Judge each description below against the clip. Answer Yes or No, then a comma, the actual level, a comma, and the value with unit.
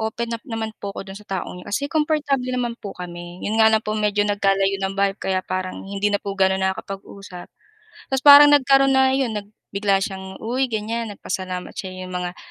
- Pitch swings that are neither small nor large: Yes, average, 3.6 semitones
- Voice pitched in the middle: No, high, 205 Hz